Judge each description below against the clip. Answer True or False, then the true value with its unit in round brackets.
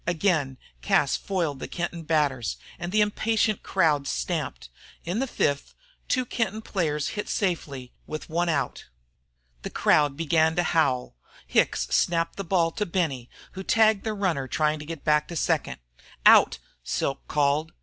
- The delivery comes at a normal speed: True (155 wpm)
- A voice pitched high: False (165 Hz)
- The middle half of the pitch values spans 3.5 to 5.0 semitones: True (4.7 semitones)